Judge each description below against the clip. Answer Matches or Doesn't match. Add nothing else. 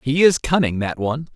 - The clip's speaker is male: Matches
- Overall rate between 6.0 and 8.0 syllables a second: Doesn't match